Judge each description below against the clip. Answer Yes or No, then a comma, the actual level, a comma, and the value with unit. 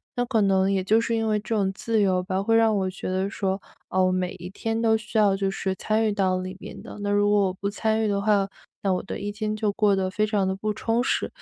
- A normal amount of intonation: No, narrow, 2.3 semitones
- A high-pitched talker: Yes, high, 205 Hz